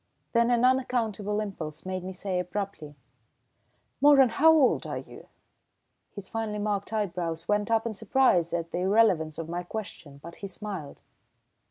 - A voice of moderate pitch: No, high, 200 Hz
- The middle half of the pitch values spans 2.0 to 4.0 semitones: No, average, 4.4 semitones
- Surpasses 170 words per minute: No, average, 155 wpm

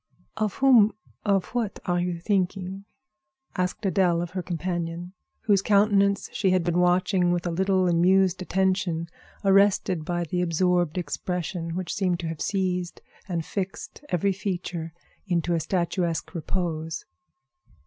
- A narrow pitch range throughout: Yes, narrow, 2.0 semitones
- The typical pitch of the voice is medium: Yes, medium, 180 Hz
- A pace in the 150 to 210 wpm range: No, slow, 135 wpm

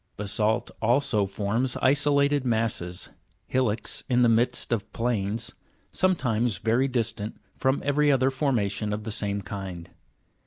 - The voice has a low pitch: Yes, low, 115 Hz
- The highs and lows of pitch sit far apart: No, average, 4.1 semitones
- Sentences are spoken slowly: Yes, slow, 125 wpm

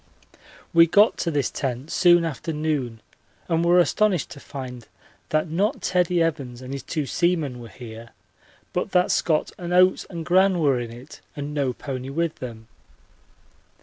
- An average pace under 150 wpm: No, average, 165 wpm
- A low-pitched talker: No, medium, 155 Hz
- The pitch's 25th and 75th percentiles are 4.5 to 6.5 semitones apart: Yes, average, 5.2 semitones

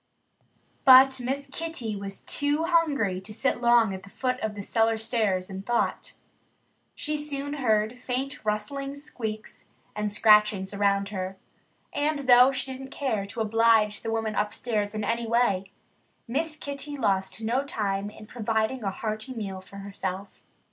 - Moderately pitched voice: No, high, 225 Hz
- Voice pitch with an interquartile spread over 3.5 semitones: Yes, average, 4.4 semitones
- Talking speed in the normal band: Yes, average, 155 wpm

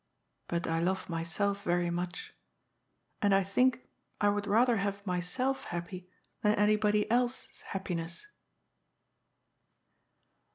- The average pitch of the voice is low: No, high, 200 Hz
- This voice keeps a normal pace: No, slow, 115 wpm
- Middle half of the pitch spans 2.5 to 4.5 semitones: Yes, average, 3.1 semitones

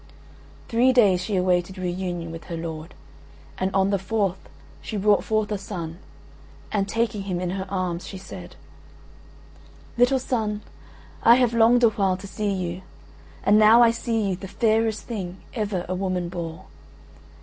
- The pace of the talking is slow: No, average, 165 wpm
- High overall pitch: Yes, high, 195 Hz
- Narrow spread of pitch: No, average, 3.2 semitones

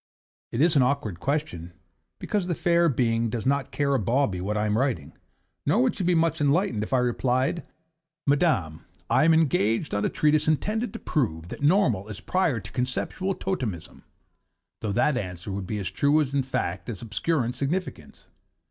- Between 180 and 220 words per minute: Yes, average, 185 wpm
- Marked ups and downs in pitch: Yes, wide, 6.6 semitones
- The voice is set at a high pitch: No, low, 130 Hz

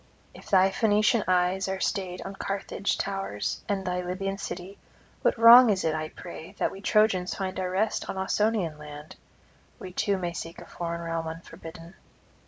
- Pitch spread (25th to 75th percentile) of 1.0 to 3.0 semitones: Yes, narrow, 2.6 semitones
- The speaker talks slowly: No, average, 175 wpm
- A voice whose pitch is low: No, medium, 185 Hz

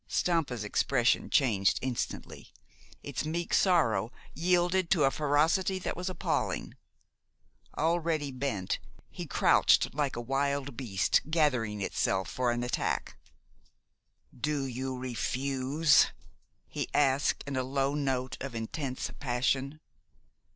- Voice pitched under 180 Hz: Yes, low, 135 Hz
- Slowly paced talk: Yes, slow, 115 wpm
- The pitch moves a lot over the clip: No, average, 3.7 semitones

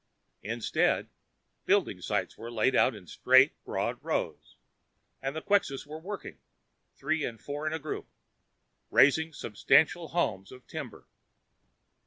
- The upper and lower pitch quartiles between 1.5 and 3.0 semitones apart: No, average, 5.1 semitones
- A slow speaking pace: Yes, slow, 125 wpm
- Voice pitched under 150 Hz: Yes, medium, 140 Hz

